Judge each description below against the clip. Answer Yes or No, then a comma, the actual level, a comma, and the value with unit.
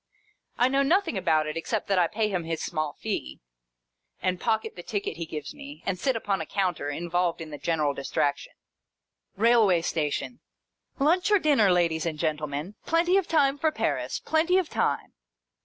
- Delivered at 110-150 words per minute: No, average, 180 wpm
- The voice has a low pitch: No, high, 195 Hz